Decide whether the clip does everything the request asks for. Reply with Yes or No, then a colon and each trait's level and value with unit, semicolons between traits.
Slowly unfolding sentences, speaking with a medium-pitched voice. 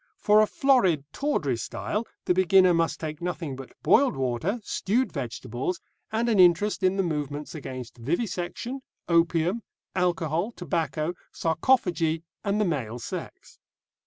Yes: slow, 130 wpm; medium, 170 Hz